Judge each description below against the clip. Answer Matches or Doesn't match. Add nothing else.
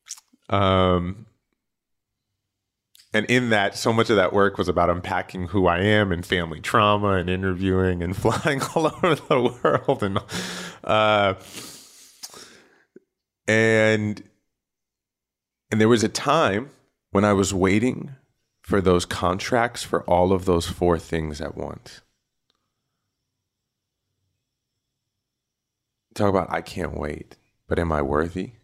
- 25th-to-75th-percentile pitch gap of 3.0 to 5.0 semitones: Matches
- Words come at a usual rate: Doesn't match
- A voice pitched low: Matches